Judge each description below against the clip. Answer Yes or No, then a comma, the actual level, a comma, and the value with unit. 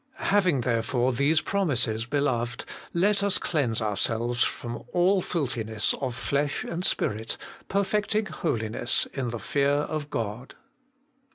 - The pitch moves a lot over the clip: Yes, wide, 6.5 semitones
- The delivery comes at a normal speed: No, slow, 125 wpm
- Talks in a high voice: No, low, 135 Hz